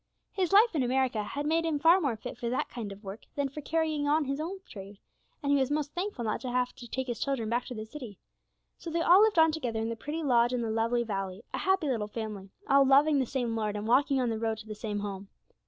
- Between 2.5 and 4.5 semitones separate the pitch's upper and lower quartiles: No, average, 5.2 semitones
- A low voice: No, very high, 250 Hz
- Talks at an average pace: No, fast, 270 wpm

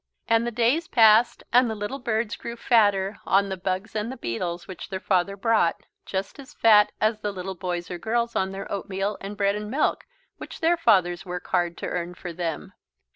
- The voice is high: Yes, high, 200 Hz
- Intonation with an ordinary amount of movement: Yes, average, 3.7 semitones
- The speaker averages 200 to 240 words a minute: Yes, fast, 205 wpm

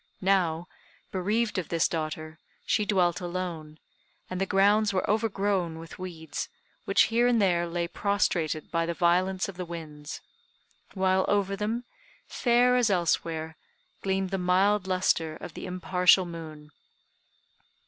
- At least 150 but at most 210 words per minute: No, average, 140 wpm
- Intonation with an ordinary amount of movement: Yes, average, 3.0 semitones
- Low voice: No, medium, 185 Hz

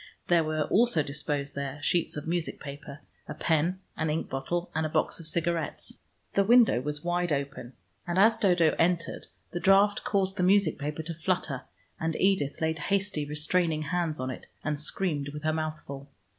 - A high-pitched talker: No, medium, 160 Hz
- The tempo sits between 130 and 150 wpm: No, average, 185 wpm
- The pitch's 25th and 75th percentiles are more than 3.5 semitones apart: No, average, 3.2 semitones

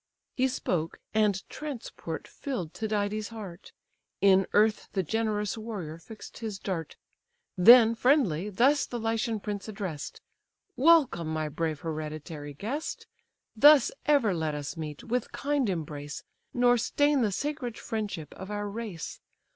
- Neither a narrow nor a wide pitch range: No, wide, 6.0 semitones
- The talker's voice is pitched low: No, high, 210 Hz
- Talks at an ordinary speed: No, slow, 130 wpm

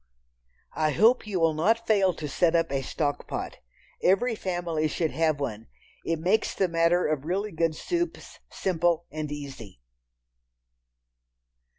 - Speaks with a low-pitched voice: No, medium, 165 Hz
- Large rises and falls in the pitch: No, average, 3.7 semitones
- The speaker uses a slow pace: No, average, 145 wpm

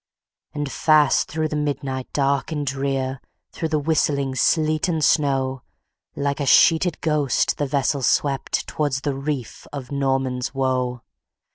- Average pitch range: No, narrow, 2.2 semitones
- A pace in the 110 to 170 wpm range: Yes, average, 140 wpm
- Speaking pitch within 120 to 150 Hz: Yes, medium, 140 Hz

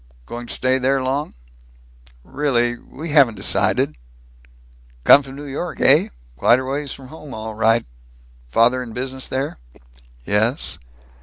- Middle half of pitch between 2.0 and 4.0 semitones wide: Yes, average, 2.7 semitones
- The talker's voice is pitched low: Yes, low, 130 Hz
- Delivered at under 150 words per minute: Yes, average, 140 wpm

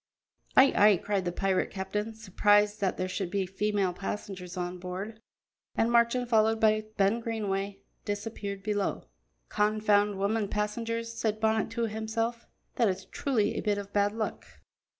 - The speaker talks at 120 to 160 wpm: Yes, average, 150 wpm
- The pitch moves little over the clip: Yes, narrow, 2.1 semitones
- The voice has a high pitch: Yes, high, 210 Hz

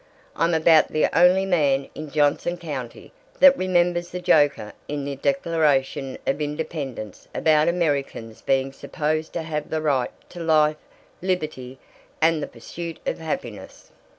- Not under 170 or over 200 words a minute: No, average, 140 wpm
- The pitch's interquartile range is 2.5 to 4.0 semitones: Yes, average, 3.4 semitones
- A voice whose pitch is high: No, medium, 155 Hz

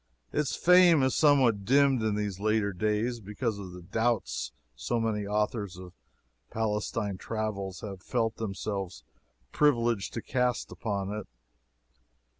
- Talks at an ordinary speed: No, slow, 130 wpm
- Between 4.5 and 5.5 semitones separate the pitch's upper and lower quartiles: No, average, 3.2 semitones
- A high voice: No, low, 110 Hz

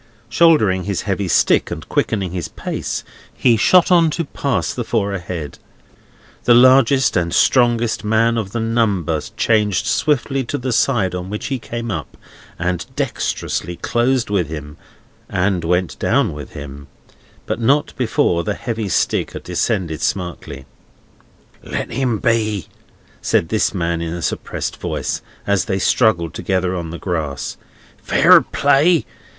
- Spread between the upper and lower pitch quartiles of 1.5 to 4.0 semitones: No, average, 5.3 semitones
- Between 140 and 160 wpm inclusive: Yes, average, 145 wpm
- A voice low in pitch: Yes, low, 100 Hz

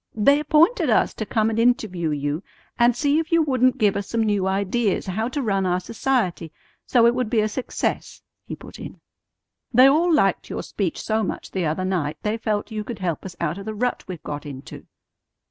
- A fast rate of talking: Yes, fast, 215 wpm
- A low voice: No, high, 215 Hz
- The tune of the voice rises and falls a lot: No, average, 4.9 semitones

